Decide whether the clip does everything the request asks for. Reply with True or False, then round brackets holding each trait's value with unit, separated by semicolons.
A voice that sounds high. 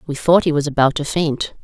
False (150 Hz)